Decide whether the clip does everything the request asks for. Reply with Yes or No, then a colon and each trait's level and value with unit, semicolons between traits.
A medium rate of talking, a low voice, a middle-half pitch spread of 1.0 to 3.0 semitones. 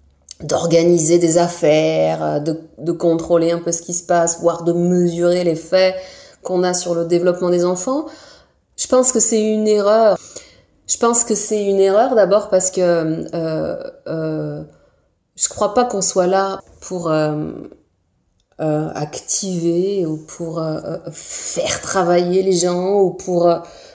No: average, 155 wpm; medium, 175 Hz; narrow, 2.6 semitones